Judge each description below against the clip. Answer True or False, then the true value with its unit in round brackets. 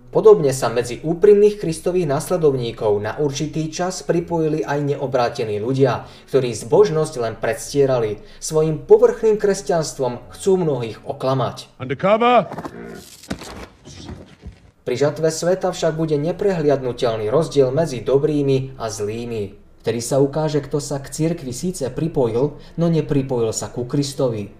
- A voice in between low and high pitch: True (145 Hz)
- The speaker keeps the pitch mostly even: False (4.9 semitones)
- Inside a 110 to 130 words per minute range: True (115 wpm)